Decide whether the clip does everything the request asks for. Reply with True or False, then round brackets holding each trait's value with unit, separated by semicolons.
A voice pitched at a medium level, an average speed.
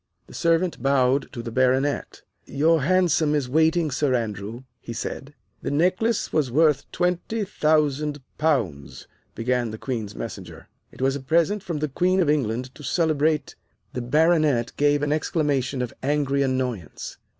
True (145 Hz; 155 wpm)